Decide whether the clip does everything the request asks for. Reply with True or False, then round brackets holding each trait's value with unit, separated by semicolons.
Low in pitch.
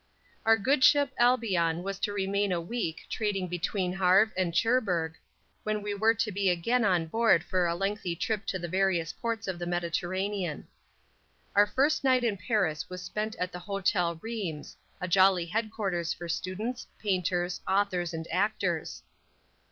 False (190 Hz)